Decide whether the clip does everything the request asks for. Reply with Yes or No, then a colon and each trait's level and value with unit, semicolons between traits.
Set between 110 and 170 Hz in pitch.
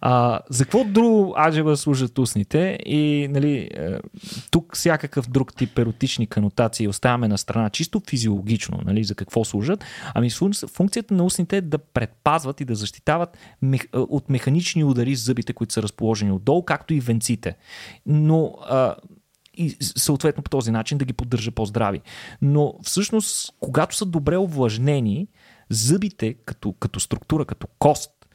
Yes: low, 135 Hz